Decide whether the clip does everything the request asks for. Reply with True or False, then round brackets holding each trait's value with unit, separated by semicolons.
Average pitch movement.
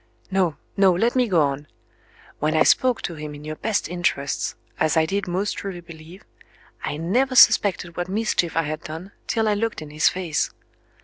True (4.5 semitones)